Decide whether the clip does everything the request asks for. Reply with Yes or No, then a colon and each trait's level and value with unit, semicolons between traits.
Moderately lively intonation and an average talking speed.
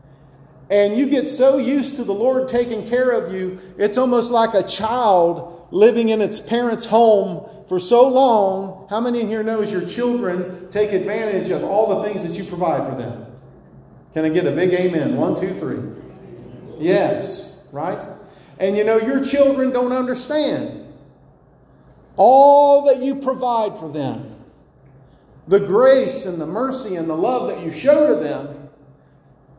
No: wide, 5.7 semitones; average, 160 wpm